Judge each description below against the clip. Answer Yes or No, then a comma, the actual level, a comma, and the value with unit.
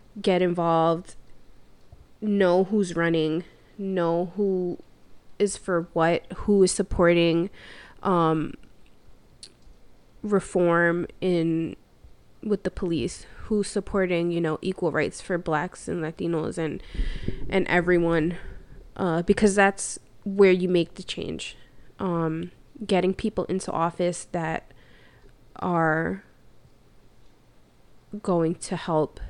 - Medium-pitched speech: Yes, medium, 175 Hz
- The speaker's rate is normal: No, slow, 100 wpm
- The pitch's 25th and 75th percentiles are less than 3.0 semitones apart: Yes, narrow, 2.5 semitones